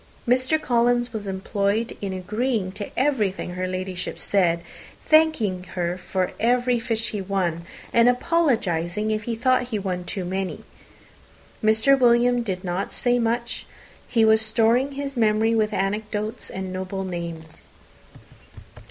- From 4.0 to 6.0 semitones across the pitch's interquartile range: Yes, average, 4.4 semitones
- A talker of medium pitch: No, high, 215 Hz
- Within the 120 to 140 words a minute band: Yes, slow, 135 wpm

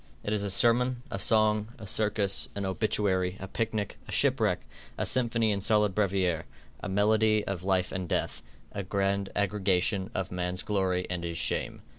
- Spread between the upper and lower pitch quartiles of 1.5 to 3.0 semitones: Yes, narrow, 2.4 semitones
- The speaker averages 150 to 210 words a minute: Yes, average, 170 wpm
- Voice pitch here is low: Yes, low, 100 Hz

